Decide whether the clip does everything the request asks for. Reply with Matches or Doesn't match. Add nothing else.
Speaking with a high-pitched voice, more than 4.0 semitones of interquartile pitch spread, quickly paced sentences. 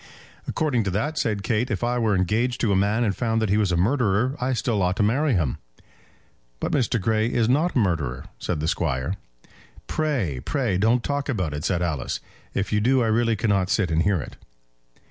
Doesn't match